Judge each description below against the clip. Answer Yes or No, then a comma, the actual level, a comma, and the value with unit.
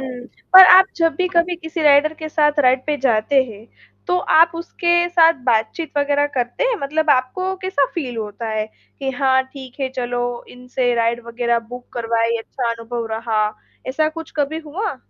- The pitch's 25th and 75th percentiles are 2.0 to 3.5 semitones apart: No, average, 5.1 semitones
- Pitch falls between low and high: No, very high, 270 Hz